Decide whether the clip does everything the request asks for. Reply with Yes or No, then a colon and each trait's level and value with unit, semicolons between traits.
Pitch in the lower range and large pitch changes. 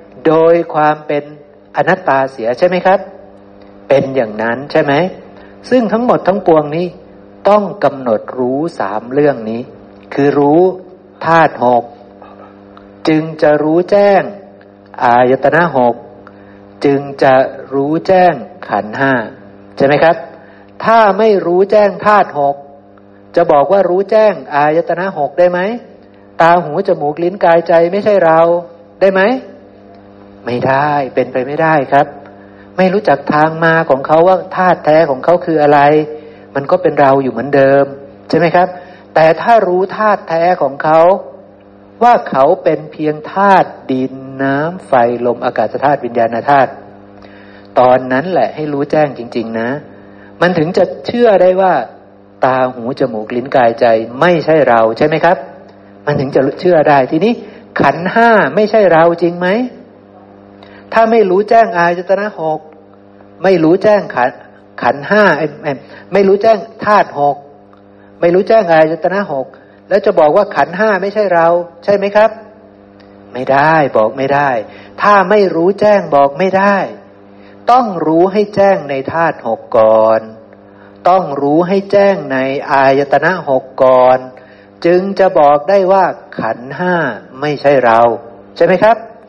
No: medium, 145 Hz; wide, 7.5 semitones